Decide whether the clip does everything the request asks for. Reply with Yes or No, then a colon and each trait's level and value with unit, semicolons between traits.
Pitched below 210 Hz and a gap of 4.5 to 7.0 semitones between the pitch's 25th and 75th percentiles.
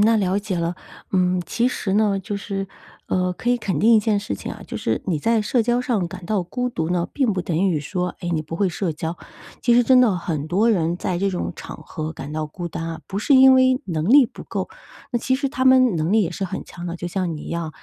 Yes: high, 190 Hz; average, 5.1 semitones